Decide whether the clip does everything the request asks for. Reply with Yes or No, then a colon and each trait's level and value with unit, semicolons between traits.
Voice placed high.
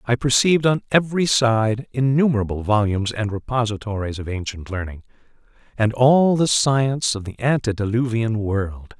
No: low, 115 Hz